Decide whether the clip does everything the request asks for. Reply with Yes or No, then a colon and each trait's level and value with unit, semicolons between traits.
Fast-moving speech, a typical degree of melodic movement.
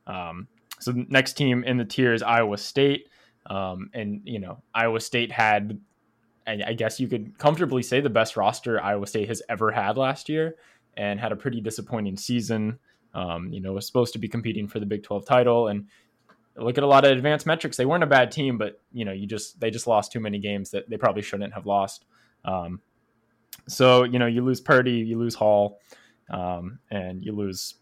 Yes: fast, 210 wpm; average, 3.4 semitones